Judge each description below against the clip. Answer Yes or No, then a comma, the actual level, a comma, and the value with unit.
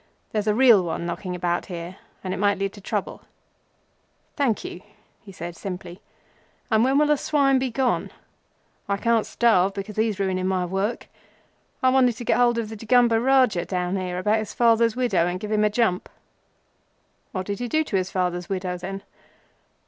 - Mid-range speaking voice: No, high, 205 Hz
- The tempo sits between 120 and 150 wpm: No, average, 185 wpm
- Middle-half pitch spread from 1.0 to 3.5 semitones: No, average, 4.3 semitones